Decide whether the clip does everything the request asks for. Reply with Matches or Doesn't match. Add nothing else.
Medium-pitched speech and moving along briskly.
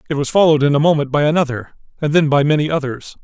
Matches